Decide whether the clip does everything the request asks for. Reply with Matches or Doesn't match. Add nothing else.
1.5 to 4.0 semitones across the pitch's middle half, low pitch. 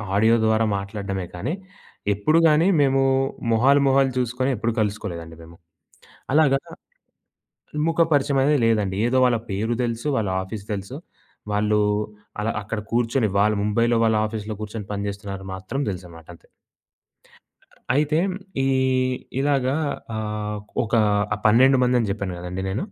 Doesn't match